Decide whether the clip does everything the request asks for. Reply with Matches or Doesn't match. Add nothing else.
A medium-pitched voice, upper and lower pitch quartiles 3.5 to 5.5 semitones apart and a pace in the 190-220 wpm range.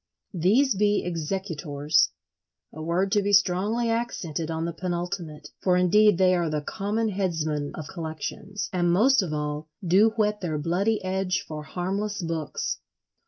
Doesn't match